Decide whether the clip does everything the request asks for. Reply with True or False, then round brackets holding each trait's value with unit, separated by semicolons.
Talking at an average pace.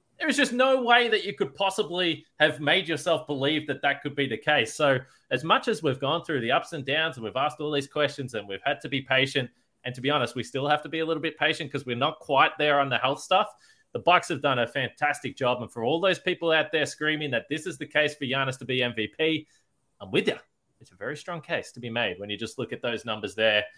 False (275 wpm)